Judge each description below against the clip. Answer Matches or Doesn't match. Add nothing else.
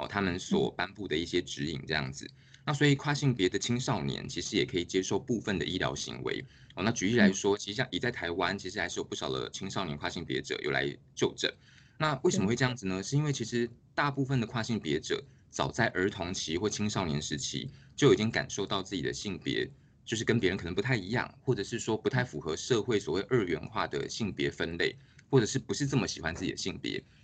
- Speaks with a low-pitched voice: Matches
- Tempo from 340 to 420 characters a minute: Matches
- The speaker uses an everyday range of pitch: Doesn't match